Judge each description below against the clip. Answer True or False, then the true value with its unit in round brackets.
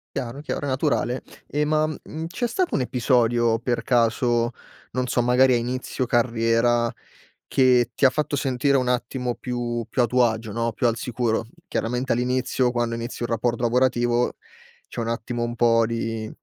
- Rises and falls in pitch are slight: True (1.5 semitones)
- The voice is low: True (120 Hz)